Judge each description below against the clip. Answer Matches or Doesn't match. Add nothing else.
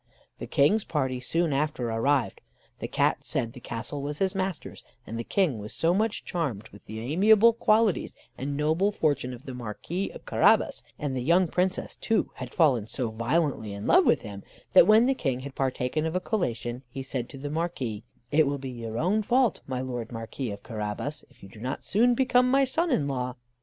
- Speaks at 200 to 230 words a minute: Matches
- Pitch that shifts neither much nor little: Doesn't match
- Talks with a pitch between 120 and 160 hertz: Matches